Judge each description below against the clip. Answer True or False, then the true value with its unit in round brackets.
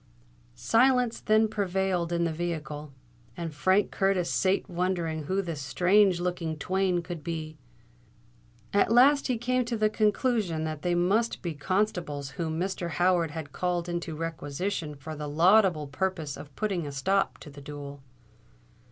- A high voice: False (175 Hz)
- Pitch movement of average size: True (3.9 semitones)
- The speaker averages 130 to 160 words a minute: True (150 wpm)